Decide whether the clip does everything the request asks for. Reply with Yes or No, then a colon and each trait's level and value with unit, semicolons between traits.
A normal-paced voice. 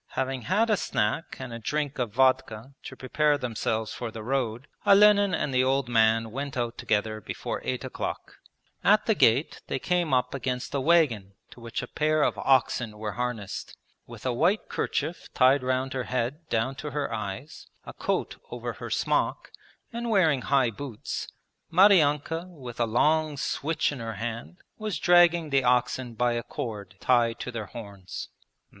Yes: average, 175 wpm